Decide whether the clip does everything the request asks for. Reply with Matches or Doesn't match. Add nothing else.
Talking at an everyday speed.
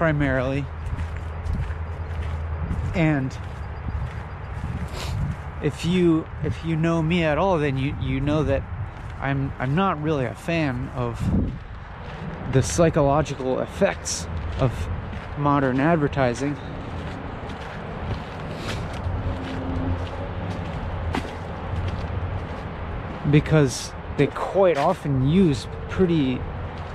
Doesn't match